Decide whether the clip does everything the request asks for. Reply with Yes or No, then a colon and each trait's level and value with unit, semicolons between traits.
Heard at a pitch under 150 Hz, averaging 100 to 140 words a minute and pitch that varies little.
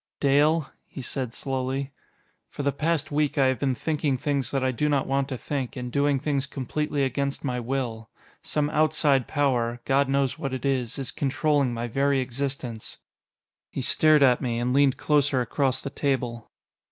No: low, 135 Hz; average, 175 wpm; narrow, 2.0 semitones